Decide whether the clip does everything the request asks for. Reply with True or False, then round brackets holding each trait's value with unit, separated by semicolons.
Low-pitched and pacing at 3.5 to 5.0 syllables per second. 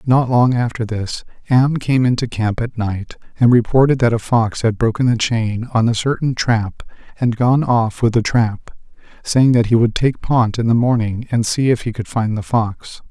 True (115 Hz; 4.6 syllables/s)